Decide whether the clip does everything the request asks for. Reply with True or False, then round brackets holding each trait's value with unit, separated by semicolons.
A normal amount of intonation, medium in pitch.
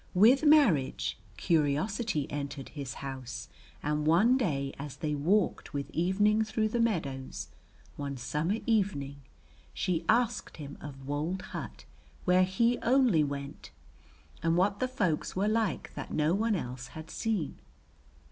False (7.1 semitones; 165 Hz)